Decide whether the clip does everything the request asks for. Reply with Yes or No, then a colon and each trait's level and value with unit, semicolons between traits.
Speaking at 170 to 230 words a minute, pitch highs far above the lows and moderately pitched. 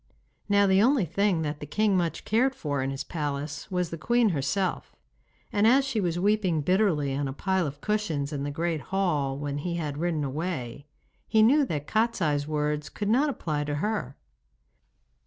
Yes: average, 185 wpm; wide, 6.0 semitones; medium, 170 Hz